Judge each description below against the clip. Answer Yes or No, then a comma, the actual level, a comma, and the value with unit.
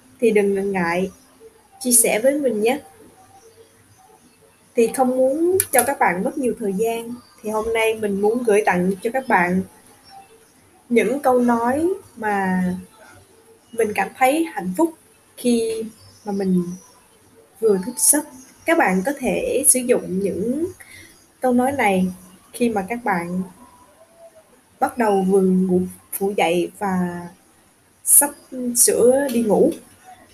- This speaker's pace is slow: Yes, slow, 135 wpm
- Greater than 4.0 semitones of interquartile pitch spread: Yes, wide, 5.6 semitones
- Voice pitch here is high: Yes, high, 235 Hz